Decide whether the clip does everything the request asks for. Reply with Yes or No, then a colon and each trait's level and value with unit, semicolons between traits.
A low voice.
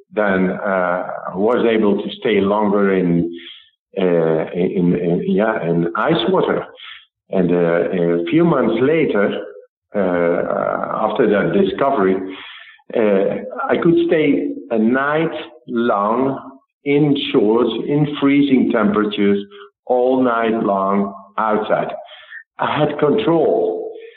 Yes: low, 105 Hz